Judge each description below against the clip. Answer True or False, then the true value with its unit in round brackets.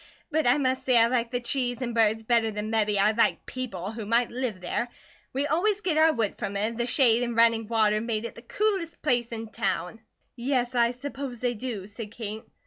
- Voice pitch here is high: True (235 Hz)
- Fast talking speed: True (225 wpm)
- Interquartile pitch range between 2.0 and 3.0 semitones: True (2.7 semitones)